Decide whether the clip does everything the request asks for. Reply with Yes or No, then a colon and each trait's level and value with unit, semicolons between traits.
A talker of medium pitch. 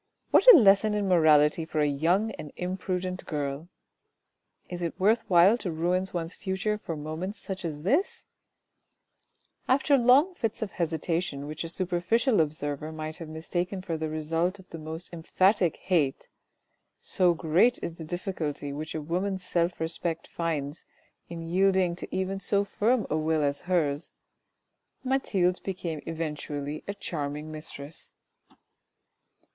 Yes: medium, 170 Hz